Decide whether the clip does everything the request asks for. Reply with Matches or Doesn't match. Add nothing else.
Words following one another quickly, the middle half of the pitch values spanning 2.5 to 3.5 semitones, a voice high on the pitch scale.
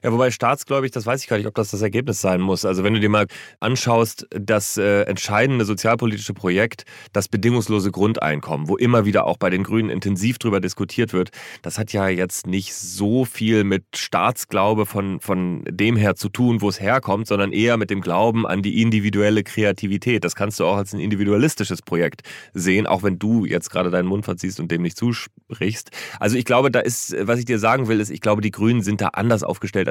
Doesn't match